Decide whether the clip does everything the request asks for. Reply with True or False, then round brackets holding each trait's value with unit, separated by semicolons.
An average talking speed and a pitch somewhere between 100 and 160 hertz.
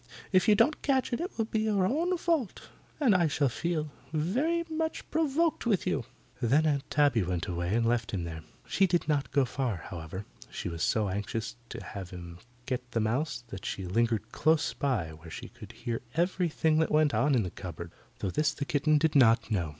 False (210 wpm; 140 Hz)